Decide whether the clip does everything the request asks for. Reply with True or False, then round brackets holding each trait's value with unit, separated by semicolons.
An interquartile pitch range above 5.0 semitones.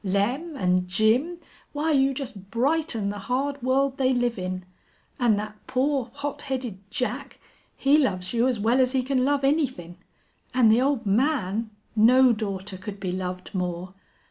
True (5.4 semitones)